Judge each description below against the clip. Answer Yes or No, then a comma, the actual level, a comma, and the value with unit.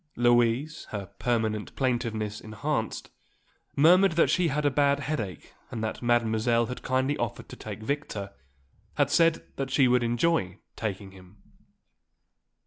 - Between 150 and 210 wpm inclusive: No, slow, 135 wpm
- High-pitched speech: No, low, 120 Hz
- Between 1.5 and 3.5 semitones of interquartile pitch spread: No, average, 4.6 semitones